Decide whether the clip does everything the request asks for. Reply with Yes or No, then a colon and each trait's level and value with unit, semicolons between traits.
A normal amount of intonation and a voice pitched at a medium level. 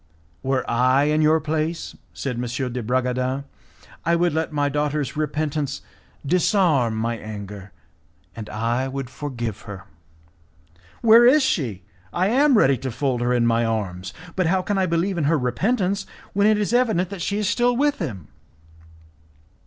No: wide, 7.1 semitones; medium, 145 Hz